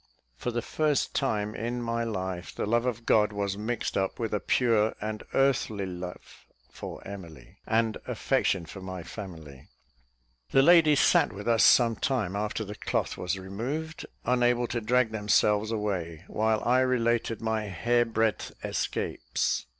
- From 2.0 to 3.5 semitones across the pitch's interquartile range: Yes, average, 3.2 semitones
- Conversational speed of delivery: Yes, average, 155 wpm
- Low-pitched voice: Yes, low, 110 Hz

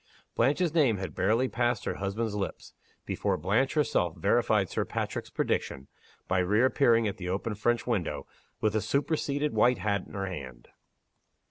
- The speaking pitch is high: No, low, 110 Hz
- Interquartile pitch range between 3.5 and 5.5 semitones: Yes, average, 4.3 semitones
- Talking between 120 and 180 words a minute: Yes, average, 155 wpm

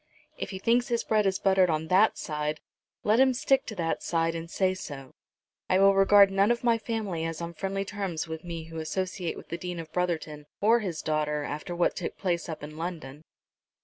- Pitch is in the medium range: Yes, medium, 180 Hz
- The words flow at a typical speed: No, fast, 215 wpm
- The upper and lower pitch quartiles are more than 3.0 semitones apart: Yes, average, 3.7 semitones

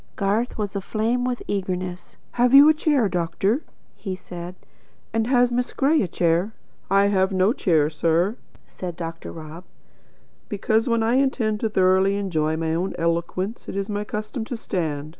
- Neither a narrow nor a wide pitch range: Yes, average, 4.6 semitones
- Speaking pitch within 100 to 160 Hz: No, high, 195 Hz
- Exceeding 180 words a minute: No, average, 165 wpm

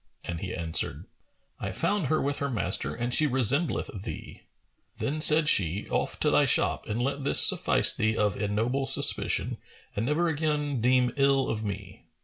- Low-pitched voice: Yes, low, 130 Hz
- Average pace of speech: Yes, average, 170 wpm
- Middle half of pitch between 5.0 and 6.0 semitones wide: Yes, average, 5.3 semitones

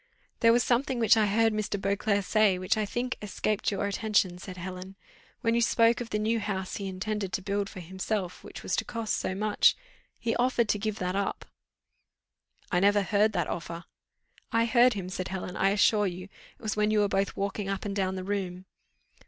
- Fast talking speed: Yes, fast, 210 wpm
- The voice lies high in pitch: Yes, high, 205 Hz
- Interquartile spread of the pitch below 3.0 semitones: Yes, narrow, 2.4 semitones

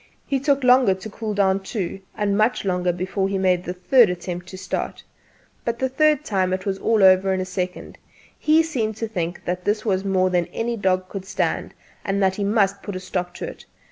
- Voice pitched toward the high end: Yes, high, 195 Hz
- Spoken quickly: Yes, fast, 220 wpm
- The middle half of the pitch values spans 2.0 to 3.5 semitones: Yes, average, 3.1 semitones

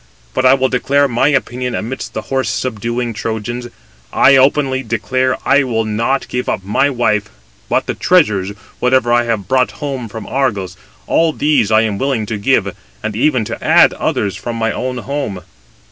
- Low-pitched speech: Yes, low, 120 Hz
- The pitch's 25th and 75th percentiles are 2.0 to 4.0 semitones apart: Yes, average, 3.3 semitones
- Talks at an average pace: Yes, average, 175 wpm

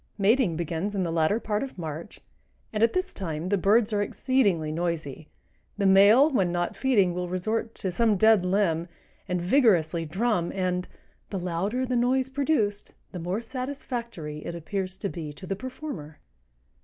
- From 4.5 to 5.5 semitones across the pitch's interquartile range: Yes, average, 5.2 semitones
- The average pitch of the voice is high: Yes, high, 195 Hz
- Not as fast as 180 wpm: Yes, average, 170 wpm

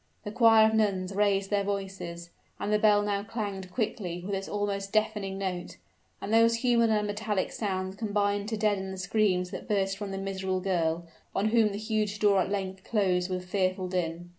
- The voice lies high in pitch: Yes, high, 200 Hz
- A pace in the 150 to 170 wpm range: No, average, 190 wpm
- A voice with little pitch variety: Yes, narrow, 2.0 semitones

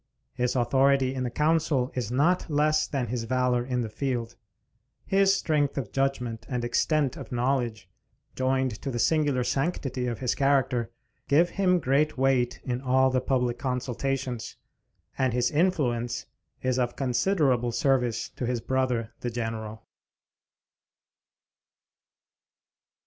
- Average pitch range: No, narrow, 2.3 semitones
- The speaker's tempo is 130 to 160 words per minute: Yes, slow, 135 wpm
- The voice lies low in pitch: Yes, low, 130 Hz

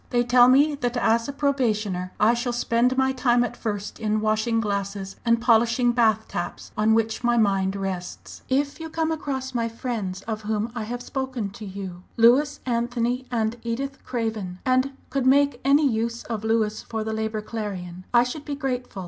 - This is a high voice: Yes, high, 235 Hz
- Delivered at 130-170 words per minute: No, average, 185 wpm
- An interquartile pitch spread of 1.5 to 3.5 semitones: Yes, average, 3.0 semitones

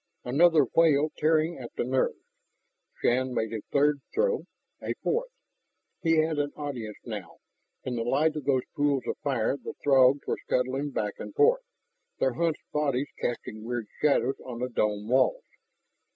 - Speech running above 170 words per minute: No, average, 160 wpm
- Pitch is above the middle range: No, medium, 140 Hz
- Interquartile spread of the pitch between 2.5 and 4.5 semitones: Yes, average, 4.0 semitones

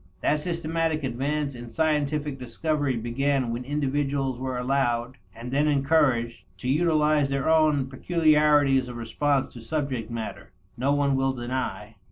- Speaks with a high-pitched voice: No, medium, 140 Hz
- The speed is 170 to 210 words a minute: No, average, 140 wpm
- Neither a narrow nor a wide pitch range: Yes, average, 3.3 semitones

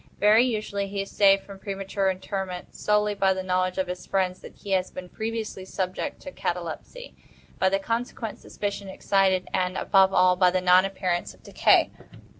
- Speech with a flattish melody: Yes, narrow, 1.7 semitones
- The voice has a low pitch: No, high, 195 Hz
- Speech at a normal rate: Yes, average, 180 wpm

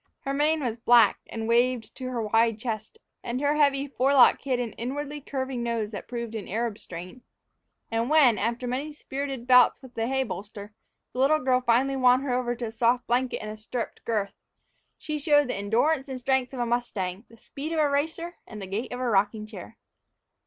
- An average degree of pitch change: Yes, average, 3.2 semitones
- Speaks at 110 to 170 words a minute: No, fast, 205 wpm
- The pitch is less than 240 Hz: No, high, 245 Hz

